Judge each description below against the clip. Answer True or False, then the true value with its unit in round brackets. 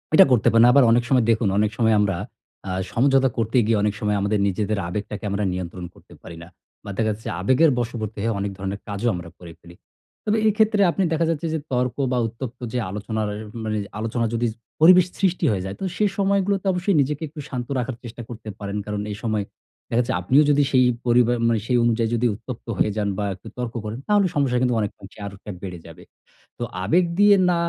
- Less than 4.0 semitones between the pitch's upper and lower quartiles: False (4.5 semitones)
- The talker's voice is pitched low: True (115 Hz)